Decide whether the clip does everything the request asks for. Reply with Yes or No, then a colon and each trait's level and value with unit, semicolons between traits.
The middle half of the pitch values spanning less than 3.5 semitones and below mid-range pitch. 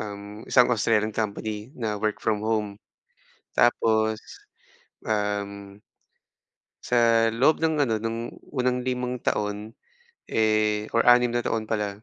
Yes: narrow, 2.4 semitones; low, 110 Hz